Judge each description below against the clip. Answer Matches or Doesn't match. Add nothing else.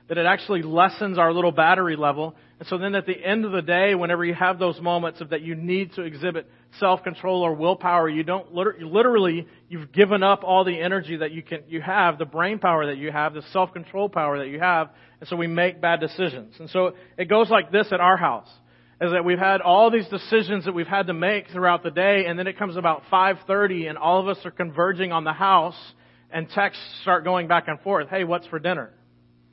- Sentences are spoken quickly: Matches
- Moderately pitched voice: Matches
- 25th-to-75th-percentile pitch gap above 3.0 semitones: Doesn't match